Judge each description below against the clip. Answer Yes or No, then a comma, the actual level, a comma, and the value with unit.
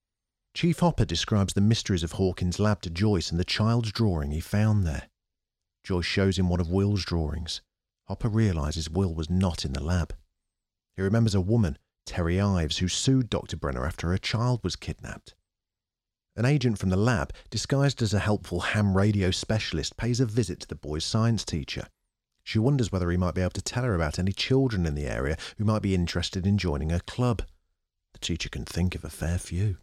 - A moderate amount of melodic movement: Yes, average, 4.3 semitones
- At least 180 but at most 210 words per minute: Yes, average, 200 wpm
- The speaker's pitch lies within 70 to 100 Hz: Yes, very low, 95 Hz